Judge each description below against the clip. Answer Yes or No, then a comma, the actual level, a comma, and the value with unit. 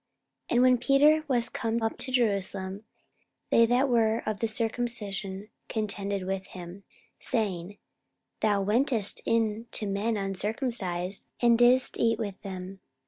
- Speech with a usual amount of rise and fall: Yes, average, 3.3 semitones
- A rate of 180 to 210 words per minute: No, average, 140 wpm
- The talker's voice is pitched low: No, high, 220 Hz